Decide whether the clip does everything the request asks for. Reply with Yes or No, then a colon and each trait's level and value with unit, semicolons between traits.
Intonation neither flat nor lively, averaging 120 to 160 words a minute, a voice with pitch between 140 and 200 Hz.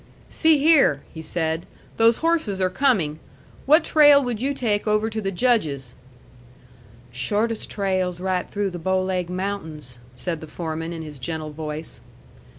No: wide, 6.0 semitones; average, 155 wpm; medium, 185 Hz